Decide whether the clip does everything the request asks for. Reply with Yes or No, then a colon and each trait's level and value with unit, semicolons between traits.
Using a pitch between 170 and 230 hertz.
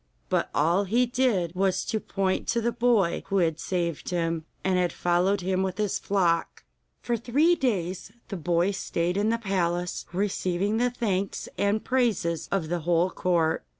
Yes: high, 190 Hz